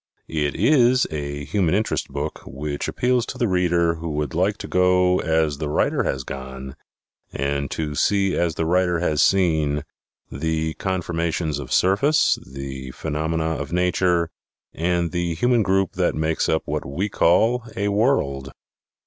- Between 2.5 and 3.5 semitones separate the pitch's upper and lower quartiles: No, average, 4.0 semitones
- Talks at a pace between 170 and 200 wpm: No, average, 155 wpm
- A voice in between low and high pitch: No, very low, 85 Hz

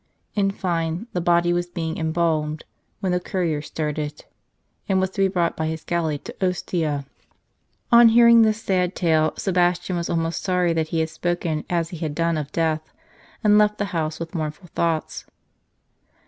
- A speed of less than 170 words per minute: No, average, 175 wpm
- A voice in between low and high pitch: Yes, medium, 170 Hz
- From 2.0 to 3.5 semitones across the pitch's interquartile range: Yes, narrow, 2.4 semitones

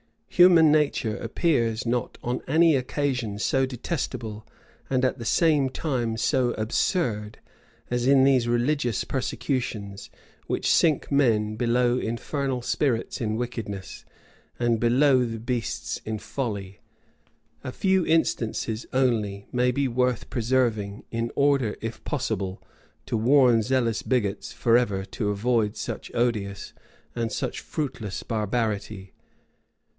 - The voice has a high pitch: No, low, 120 Hz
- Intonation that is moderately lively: Yes, average, 3.3 semitones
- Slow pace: Yes, slow, 120 wpm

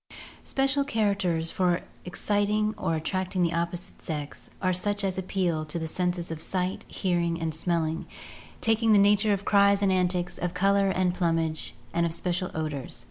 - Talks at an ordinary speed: Yes, average, 165 wpm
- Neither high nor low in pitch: Yes, medium, 180 Hz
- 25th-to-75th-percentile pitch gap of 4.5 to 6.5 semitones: No, average, 3.0 semitones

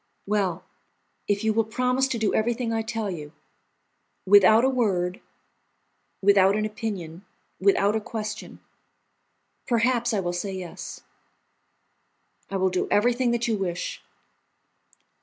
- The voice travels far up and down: No, average, 3.4 semitones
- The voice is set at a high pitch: Yes, high, 210 Hz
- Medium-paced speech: No, slow, 125 wpm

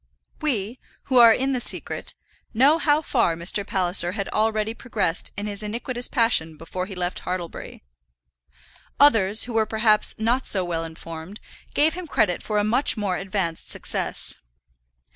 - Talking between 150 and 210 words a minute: Yes, average, 155 wpm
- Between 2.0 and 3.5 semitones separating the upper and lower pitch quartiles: No, average, 4.8 semitones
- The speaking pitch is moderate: No, high, 210 Hz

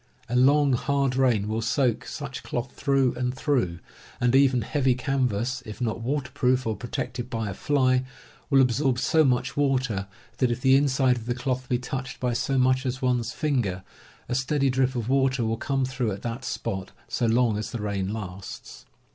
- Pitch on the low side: Yes, low, 125 Hz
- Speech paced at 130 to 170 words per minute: No, average, 195 wpm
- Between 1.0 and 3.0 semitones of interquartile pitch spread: Yes, narrow, 2.4 semitones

